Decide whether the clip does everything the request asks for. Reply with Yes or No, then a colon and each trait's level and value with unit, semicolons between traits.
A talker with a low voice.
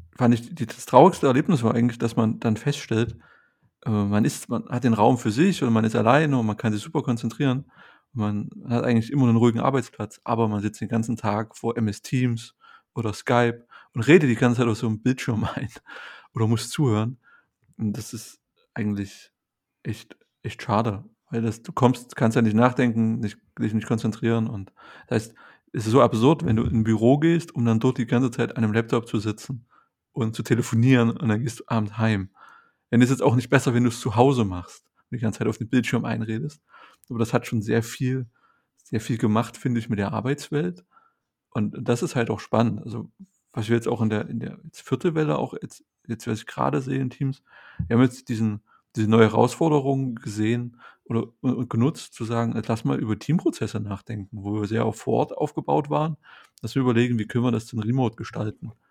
Yes: low, 115 Hz